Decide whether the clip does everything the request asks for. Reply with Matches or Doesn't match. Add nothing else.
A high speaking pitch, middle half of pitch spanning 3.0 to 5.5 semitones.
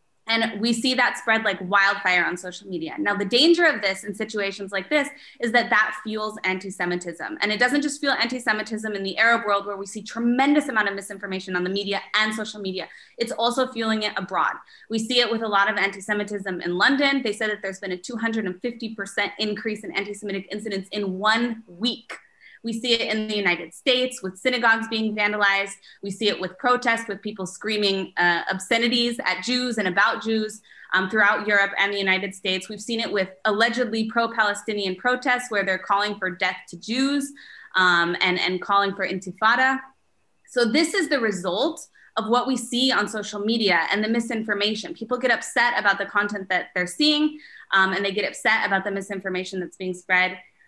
Matches